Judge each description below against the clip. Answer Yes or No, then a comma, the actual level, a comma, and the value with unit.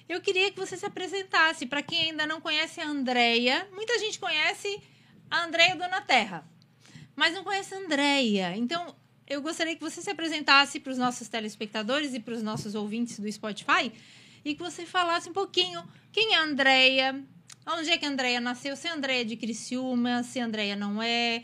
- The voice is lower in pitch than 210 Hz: No, very high, 285 Hz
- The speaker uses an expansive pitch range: Yes, wide, 6.2 semitones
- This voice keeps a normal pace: No, fast, 195 wpm